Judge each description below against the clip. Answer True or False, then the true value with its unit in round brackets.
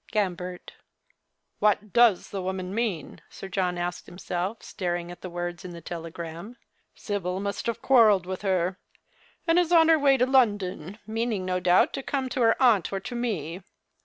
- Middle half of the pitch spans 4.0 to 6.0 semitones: True (4.6 semitones)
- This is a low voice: False (195 Hz)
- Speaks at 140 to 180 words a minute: False (190 wpm)